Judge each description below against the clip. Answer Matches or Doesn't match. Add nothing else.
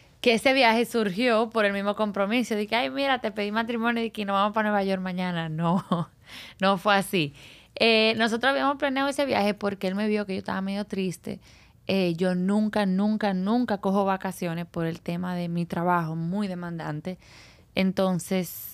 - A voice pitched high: Matches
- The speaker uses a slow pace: Doesn't match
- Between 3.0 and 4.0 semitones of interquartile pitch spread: Matches